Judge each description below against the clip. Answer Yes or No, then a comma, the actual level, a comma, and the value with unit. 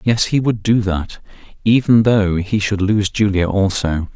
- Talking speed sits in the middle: Yes, average, 175 wpm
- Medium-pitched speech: No, low, 100 Hz